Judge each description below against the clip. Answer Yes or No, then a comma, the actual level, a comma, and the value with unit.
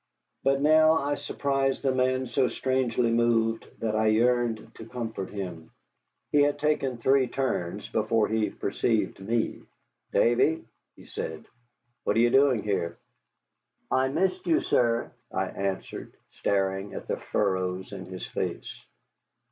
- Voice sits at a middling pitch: No, low, 120 Hz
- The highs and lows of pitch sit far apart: No, average, 4.6 semitones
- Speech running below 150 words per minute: Yes, average, 140 wpm